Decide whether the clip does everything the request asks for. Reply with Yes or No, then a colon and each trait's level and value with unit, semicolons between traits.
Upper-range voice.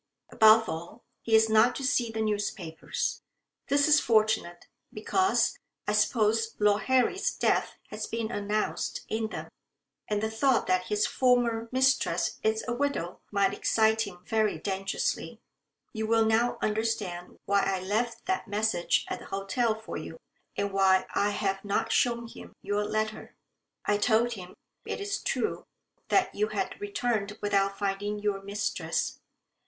Yes: high, 220 Hz